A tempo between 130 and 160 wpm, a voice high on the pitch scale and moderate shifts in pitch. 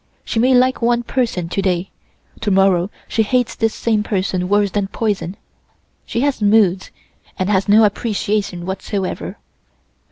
Yes: average, 150 wpm; high, 205 Hz; average, 3.1 semitones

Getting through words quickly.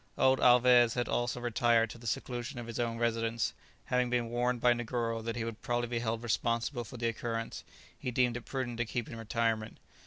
Yes: fast, 210 wpm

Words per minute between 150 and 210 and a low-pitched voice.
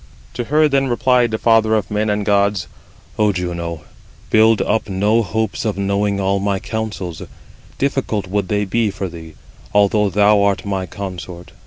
Yes: average, 165 wpm; low, 105 Hz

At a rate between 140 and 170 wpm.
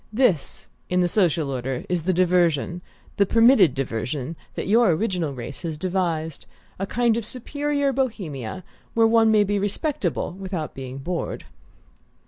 Yes: average, 145 wpm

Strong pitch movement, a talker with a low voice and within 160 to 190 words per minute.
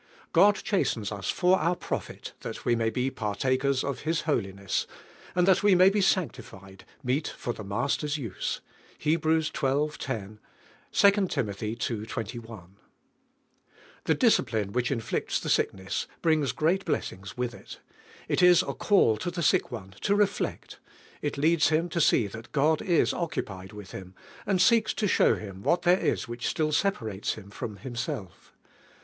Yes: wide, 7.9 semitones; low, 130 Hz; average, 165 wpm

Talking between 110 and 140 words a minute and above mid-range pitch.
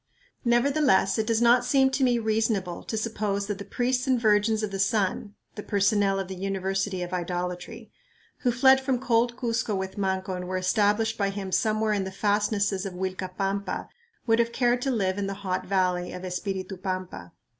No: average, 190 wpm; high, 205 Hz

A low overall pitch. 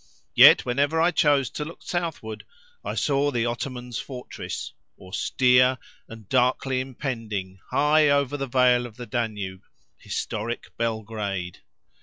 Yes: low, 125 Hz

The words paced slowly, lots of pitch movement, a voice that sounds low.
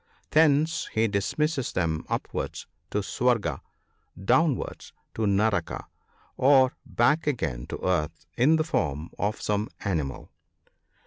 Yes: slow, 115 wpm; wide, 7.7 semitones; low, 110 Hz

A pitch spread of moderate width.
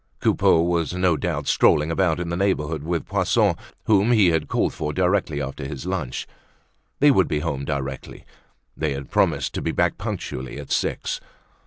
Yes: average, 3.7 semitones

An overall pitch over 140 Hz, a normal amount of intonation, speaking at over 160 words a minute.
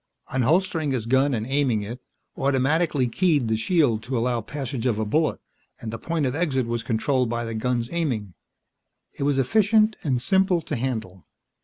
No: low, 130 Hz; average, 4.6 semitones; average, 175 wpm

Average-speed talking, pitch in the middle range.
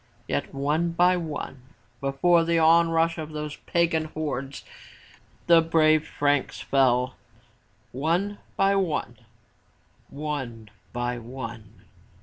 No: slow, 110 wpm; medium, 150 Hz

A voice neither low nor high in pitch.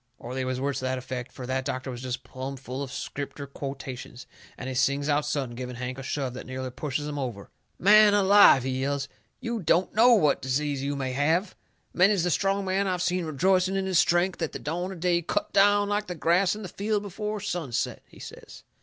Yes: medium, 150 Hz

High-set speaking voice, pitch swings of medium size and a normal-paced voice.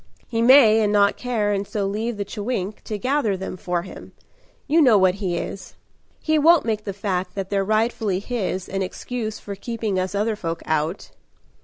Yes: high, 205 Hz; average, 3.1 semitones; average, 190 wpm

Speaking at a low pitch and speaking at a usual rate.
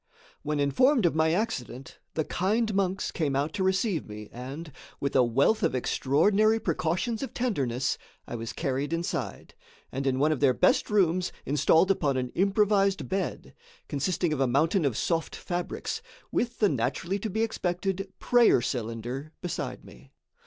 No: medium, 160 Hz; average, 160 wpm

